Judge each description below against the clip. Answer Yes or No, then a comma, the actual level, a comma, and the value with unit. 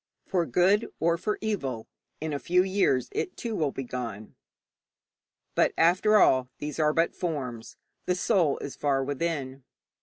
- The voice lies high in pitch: No, medium, 155 Hz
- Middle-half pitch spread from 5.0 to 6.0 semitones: Yes, average, 5.3 semitones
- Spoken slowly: No, average, 155 wpm